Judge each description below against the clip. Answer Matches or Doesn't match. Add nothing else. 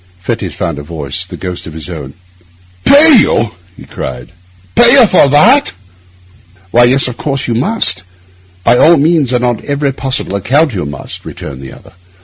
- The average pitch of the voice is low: Matches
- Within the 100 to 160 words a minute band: Doesn't match